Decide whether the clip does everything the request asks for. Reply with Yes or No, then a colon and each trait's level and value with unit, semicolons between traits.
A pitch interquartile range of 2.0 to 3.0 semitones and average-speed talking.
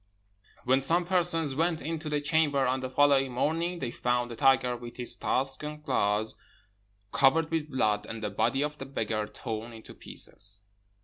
No: average, 4.2 semitones; average, 175 wpm